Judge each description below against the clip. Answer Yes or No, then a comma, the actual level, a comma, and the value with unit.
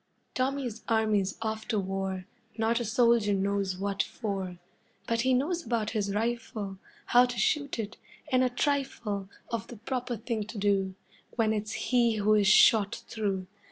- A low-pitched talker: No, high, 220 Hz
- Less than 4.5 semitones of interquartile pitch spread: Yes, average, 3.1 semitones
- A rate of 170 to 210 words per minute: No, average, 160 wpm